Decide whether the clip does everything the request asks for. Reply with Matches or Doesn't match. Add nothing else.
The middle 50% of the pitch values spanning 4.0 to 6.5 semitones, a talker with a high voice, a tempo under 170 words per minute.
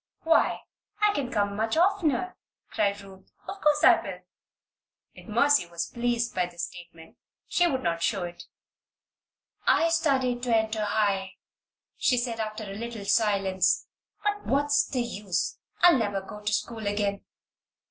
Matches